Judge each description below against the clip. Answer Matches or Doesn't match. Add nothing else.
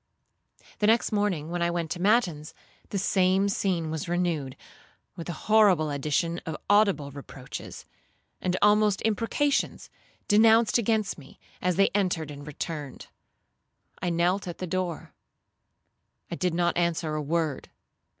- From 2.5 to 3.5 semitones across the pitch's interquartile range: Doesn't match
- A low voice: Doesn't match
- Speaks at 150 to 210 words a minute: Doesn't match